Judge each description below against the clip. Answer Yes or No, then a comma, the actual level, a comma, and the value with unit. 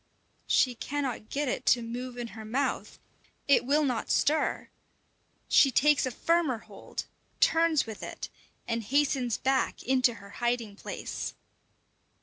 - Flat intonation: No, average, 3.4 semitones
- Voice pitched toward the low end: No, very high, 255 Hz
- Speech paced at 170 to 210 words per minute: No, slow, 135 wpm